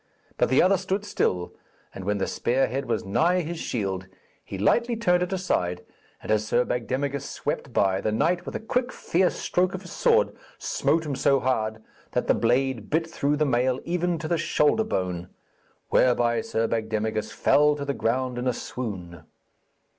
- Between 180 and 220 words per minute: Yes, average, 185 wpm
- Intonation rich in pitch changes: Yes, wide, 7.8 semitones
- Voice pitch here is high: No, low, 130 Hz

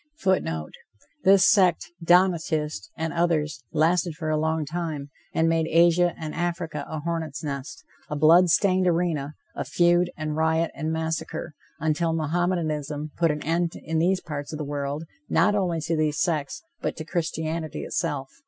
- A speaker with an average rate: Yes, average, 160 wpm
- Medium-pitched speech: Yes, medium, 160 Hz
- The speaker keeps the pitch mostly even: Yes, narrow, 2.2 semitones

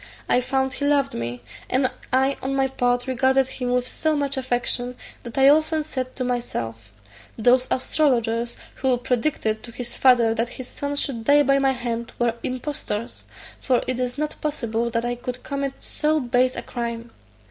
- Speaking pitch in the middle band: No, very high, 255 Hz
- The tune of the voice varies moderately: No, narrow, 2.3 semitones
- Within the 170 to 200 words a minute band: Yes, average, 180 wpm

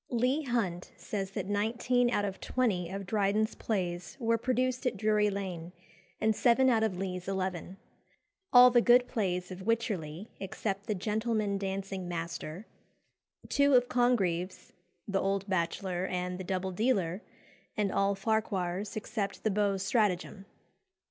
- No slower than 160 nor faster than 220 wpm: No, average, 140 wpm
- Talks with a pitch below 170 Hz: No, high, 200 Hz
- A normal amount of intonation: Yes, average, 3.5 semitones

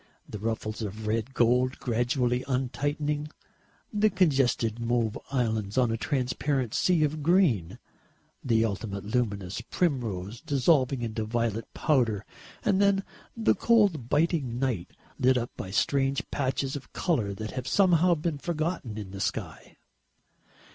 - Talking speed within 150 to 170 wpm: No, slow, 135 wpm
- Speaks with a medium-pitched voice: No, low, 125 Hz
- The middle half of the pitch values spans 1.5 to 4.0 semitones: No, average, 5.0 semitones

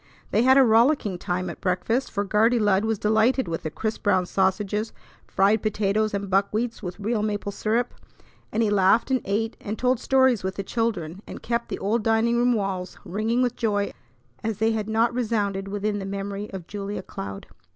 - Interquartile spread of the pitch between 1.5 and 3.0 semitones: Yes, narrow, 2.6 semitones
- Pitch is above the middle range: Yes, high, 210 Hz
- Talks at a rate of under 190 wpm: No, average, 195 wpm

